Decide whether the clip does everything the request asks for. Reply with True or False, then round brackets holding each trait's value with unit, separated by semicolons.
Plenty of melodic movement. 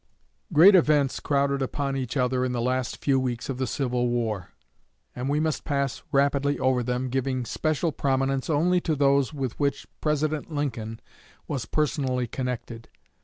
False (2.4 semitones)